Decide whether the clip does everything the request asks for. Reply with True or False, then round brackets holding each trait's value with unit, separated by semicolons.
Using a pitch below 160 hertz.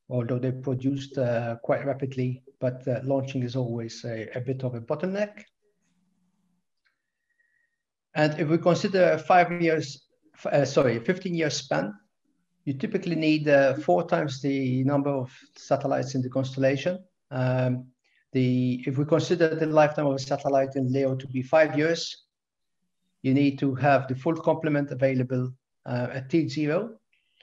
True (140 Hz)